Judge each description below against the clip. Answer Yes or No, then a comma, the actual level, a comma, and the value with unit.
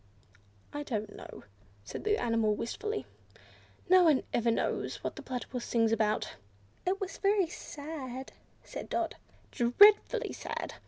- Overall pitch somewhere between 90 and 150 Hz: No, very high, 260 Hz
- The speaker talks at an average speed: No, slow, 130 wpm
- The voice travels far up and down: Yes, wide, 8.3 semitones